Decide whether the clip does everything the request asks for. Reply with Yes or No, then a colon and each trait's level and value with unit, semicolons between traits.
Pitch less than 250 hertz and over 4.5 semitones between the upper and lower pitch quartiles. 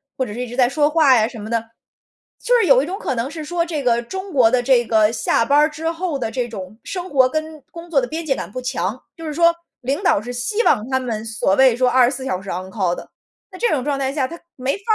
No: very high, 260 Hz; average, 5.1 semitones